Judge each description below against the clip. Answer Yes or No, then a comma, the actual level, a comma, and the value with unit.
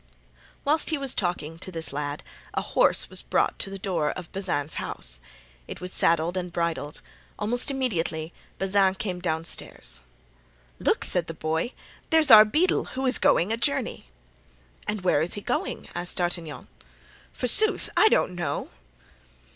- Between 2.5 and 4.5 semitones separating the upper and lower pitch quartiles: No, average, 5.0 semitones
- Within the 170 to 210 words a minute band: No, average, 155 wpm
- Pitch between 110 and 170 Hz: No, medium, 180 Hz